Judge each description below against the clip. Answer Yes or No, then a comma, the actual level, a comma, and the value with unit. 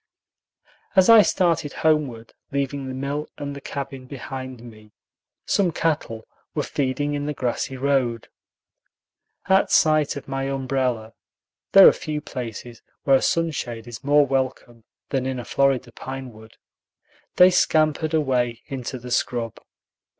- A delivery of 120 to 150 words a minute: Yes, average, 140 wpm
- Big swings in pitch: No, average, 3.1 semitones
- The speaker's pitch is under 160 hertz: Yes, low, 135 Hz